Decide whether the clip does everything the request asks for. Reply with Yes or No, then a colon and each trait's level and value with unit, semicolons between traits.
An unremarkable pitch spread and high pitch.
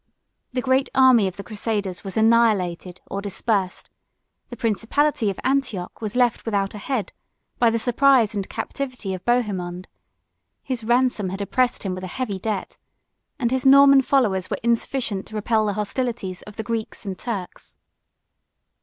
Yes: average, 4.1 semitones; high, 220 Hz